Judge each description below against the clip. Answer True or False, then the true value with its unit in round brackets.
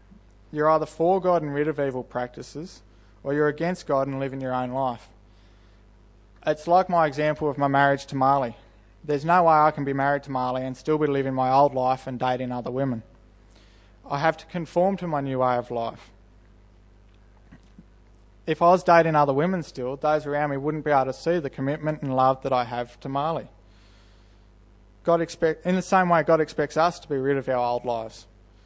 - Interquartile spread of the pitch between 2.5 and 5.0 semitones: False (5.6 semitones)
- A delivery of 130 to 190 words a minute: False (205 wpm)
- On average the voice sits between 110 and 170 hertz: True (135 Hz)